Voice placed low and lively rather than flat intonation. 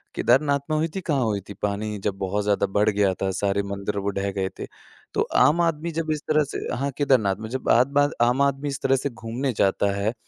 Yes: low, 115 Hz; wide, 5.9 semitones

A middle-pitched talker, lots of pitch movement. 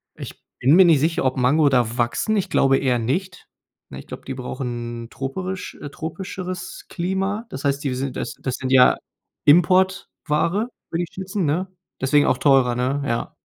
Yes: medium, 145 Hz; wide, 6.0 semitones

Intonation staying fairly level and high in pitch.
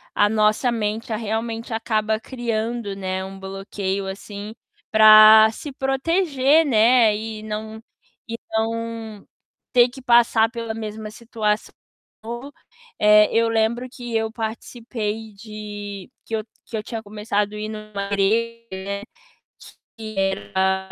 Yes: narrow, 1.7 semitones; high, 220 Hz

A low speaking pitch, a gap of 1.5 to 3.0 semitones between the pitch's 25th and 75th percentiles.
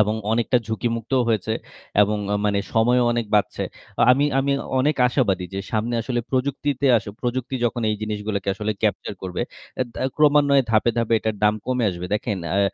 No: low, 115 Hz; average, 3.4 semitones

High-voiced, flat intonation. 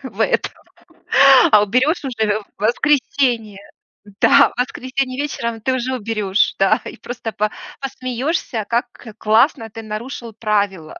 No: high, 230 Hz; average, 3.3 semitones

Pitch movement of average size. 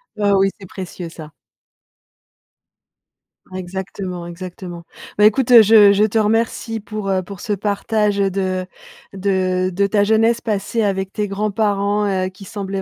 No: narrow, 2.1 semitones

